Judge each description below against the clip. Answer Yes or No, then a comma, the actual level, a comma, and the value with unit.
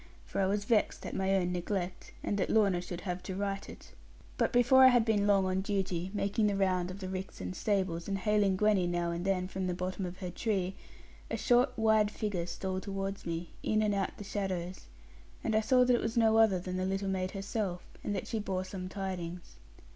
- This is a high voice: Yes, high, 195 Hz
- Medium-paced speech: No, fast, 225 wpm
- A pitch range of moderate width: No, narrow, 2.2 semitones